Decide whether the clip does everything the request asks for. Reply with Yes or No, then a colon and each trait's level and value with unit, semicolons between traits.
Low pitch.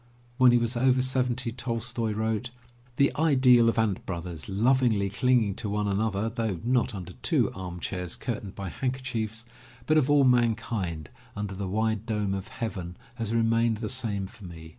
Yes: low, 110 Hz